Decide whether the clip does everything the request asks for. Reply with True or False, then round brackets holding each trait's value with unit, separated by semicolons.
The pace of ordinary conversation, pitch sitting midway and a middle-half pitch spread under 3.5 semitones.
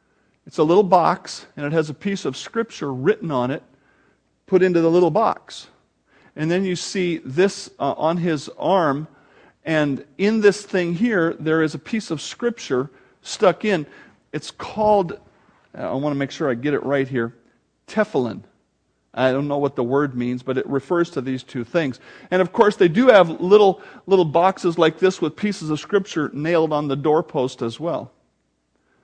False (185 wpm; 160 Hz; 5.3 semitones)